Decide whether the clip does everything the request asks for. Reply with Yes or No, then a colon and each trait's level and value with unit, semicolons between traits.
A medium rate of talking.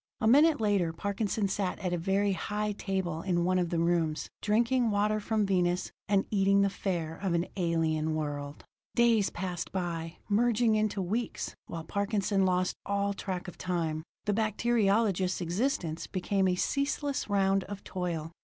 Yes: average, 160 wpm